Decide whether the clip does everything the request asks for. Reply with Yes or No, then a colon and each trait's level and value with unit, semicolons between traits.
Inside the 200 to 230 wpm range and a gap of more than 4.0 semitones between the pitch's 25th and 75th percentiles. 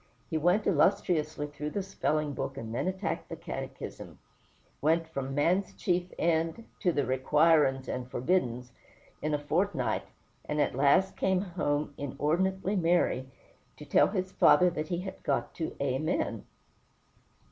No: average, 145 wpm; average, 4.4 semitones